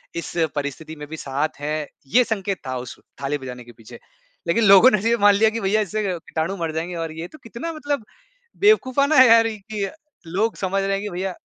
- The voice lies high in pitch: Yes, high, 195 Hz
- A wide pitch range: Yes, wide, 6.1 semitones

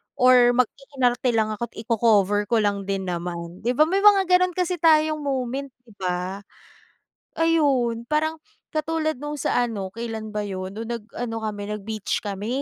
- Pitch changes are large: Yes, wide, 6.2 semitones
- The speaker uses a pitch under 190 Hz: No, high, 235 Hz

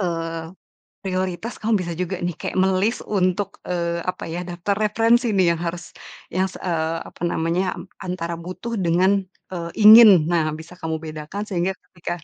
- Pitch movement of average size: No, narrow, 2.3 semitones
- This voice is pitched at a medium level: Yes, medium, 180 Hz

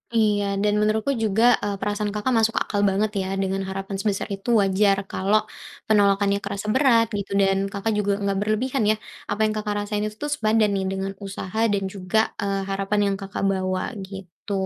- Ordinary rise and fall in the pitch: No, narrow, 1.6 semitones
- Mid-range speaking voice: No, high, 205 Hz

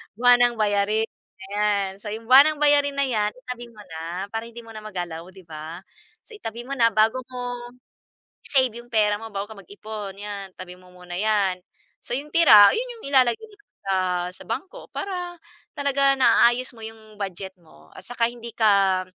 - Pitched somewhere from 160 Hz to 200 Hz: No, high, 220 Hz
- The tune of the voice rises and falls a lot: No, average, 4.2 semitones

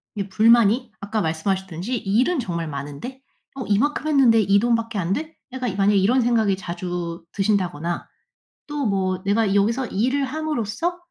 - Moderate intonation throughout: Yes, average, 4.8 semitones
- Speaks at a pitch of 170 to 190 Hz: No, high, 210 Hz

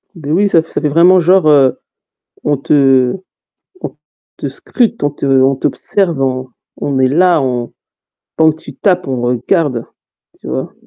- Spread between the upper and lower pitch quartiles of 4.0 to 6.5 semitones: Yes, average, 4.4 semitones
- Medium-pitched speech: Yes, medium, 145 Hz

